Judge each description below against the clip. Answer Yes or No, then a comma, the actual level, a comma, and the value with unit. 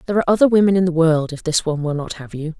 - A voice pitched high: No, medium, 170 Hz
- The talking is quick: Yes, fast, 325 wpm